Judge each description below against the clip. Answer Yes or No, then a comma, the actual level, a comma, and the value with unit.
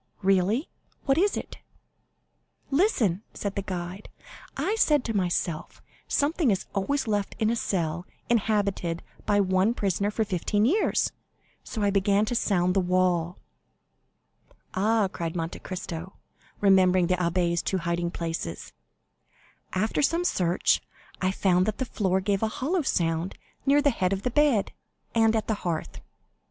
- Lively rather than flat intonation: No, average, 3.8 semitones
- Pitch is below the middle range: No, high, 195 Hz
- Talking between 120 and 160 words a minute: Yes, average, 145 wpm